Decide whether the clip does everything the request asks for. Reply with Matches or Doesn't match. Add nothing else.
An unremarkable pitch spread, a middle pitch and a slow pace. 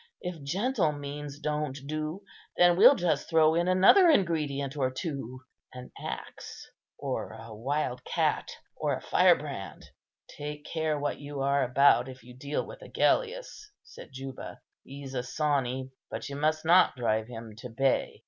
Doesn't match